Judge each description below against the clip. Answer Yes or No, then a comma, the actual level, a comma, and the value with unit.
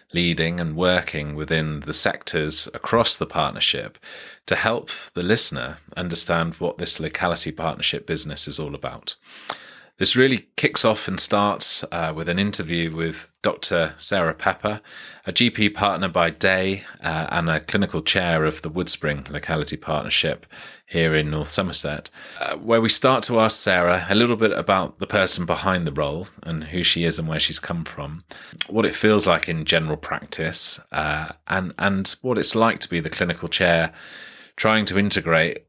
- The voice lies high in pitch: No, very low, 85 Hz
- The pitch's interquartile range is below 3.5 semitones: No, average, 4.1 semitones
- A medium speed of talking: Yes, average, 170 wpm